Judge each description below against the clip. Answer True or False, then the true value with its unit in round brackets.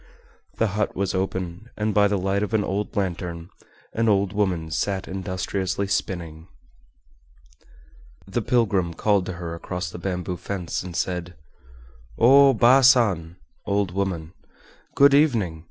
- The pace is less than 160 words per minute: True (140 wpm)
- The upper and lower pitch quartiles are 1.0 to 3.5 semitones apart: True (2.9 semitones)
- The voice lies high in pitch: False (95 Hz)